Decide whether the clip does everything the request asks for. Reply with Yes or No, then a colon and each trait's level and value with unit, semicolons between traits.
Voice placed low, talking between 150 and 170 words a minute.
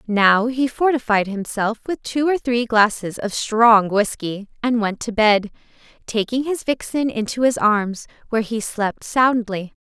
No: high, 225 Hz; average, 160 wpm